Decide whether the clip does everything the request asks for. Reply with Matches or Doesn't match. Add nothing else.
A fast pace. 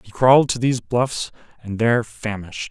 Doesn't match